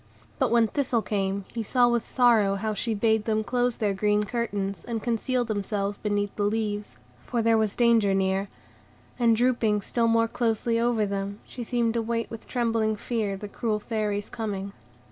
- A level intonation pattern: Yes, narrow, 2.3 semitones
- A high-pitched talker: Yes, high, 220 Hz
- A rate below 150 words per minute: No, average, 180 wpm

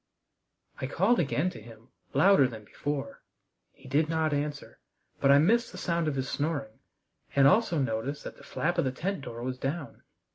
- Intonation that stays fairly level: No, average, 4.0 semitones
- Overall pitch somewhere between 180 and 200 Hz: No, medium, 145 Hz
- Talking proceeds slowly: No, average, 185 wpm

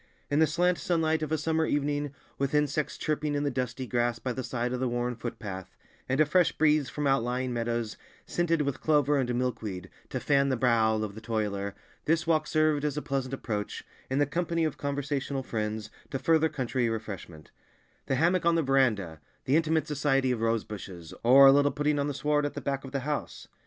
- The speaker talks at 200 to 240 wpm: Yes, fast, 205 wpm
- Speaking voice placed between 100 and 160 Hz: Yes, low, 135 Hz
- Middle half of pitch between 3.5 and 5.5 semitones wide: Yes, average, 4.0 semitones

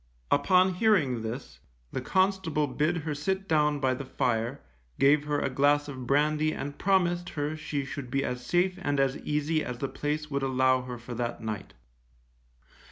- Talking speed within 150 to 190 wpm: Yes, average, 175 wpm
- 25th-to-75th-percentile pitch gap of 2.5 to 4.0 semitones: Yes, average, 3.3 semitones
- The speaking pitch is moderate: Yes, medium, 145 Hz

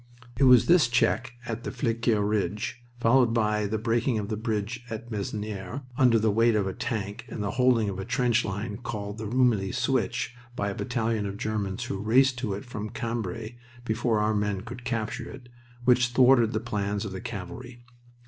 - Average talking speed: Yes, average, 190 wpm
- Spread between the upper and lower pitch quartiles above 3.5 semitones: No, average, 2.7 semitones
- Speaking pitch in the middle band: No, low, 110 Hz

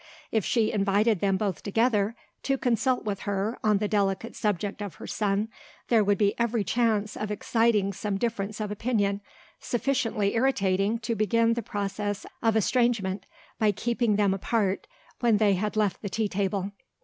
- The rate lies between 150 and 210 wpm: Yes, average, 165 wpm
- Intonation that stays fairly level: Yes, narrow, 2.3 semitones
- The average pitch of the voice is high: Yes, high, 210 Hz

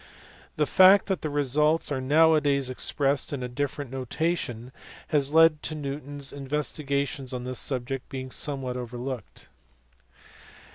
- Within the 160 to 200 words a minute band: No, average, 145 wpm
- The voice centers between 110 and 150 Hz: Yes, medium, 140 Hz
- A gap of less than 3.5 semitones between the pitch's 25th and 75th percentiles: Yes, narrow, 2.6 semitones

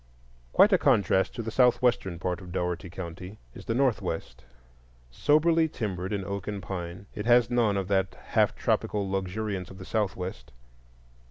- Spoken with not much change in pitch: No, average, 3.7 semitones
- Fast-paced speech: No, average, 160 wpm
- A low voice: Yes, low, 100 Hz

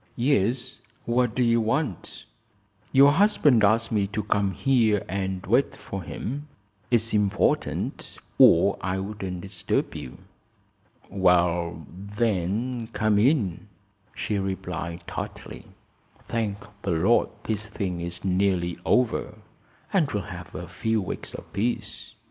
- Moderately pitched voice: No, low, 105 Hz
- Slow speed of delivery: Yes, slow, 125 wpm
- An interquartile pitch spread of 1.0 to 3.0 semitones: No, average, 4.1 semitones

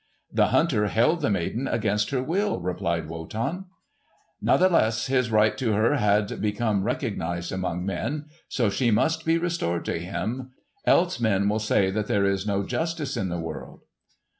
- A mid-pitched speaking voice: No, low, 110 Hz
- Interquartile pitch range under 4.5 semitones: No, wide, 5.4 semitones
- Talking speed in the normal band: Yes, average, 165 wpm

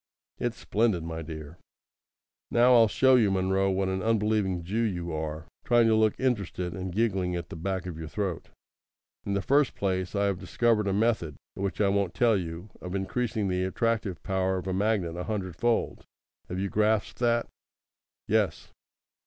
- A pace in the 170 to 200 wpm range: Yes, average, 180 wpm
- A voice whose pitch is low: Yes, very low, 95 Hz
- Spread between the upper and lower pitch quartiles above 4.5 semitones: No, average, 3.5 semitones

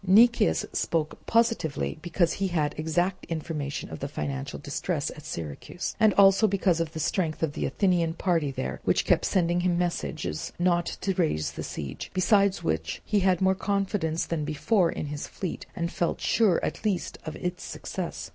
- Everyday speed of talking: Yes, average, 175 wpm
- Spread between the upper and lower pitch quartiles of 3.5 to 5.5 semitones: Yes, average, 3.8 semitones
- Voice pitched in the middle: Yes, medium, 175 Hz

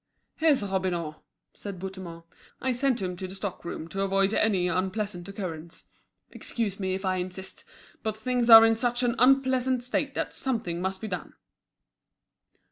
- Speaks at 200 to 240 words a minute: No, average, 160 wpm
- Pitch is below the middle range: No, high, 195 Hz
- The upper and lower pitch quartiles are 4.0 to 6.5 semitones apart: Yes, average, 4.5 semitones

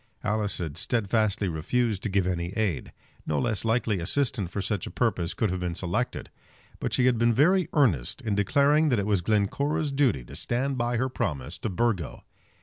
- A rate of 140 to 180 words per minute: No, average, 190 wpm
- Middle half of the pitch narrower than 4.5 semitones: No, average, 5.1 semitones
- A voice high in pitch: No, low, 110 Hz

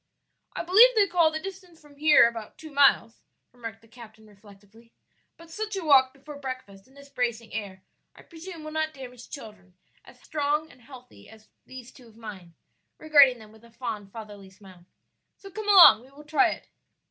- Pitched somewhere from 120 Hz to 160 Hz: No, very high, 255 Hz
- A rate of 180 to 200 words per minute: Yes, average, 190 wpm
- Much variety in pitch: Yes, wide, 6.1 semitones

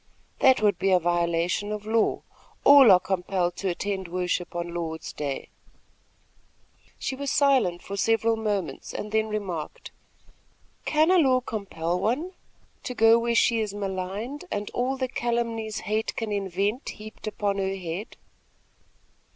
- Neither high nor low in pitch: No, high, 210 Hz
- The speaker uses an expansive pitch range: No, average, 4.2 semitones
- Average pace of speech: Yes, average, 145 wpm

